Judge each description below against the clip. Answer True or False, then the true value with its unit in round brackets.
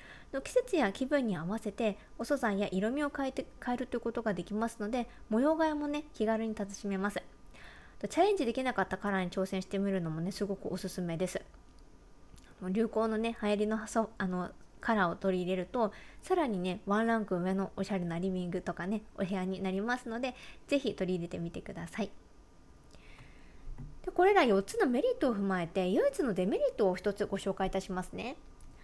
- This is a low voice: False (210 Hz)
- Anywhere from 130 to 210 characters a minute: False (380 characters per minute)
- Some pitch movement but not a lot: True (4.3 semitones)